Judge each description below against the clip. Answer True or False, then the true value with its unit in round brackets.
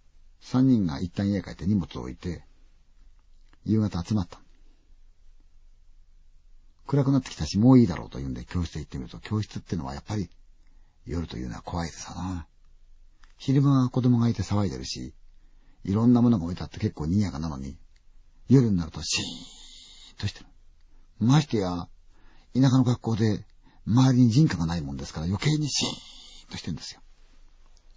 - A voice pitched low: True (85 Hz)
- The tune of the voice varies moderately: False (6.2 semitones)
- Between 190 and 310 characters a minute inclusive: False (345 characters per minute)